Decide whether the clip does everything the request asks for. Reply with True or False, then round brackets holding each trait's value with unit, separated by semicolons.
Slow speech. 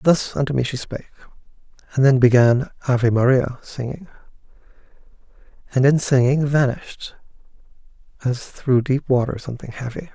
True (125 wpm)